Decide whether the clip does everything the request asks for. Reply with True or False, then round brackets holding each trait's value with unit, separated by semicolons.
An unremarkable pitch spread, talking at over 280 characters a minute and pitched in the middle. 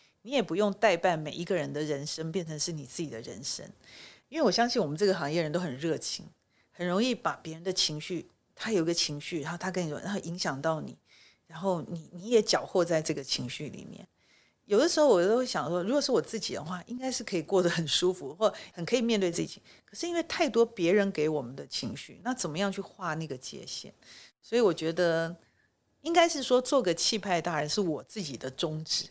True (4.8 semitones; 330 characters per minute; 180 Hz)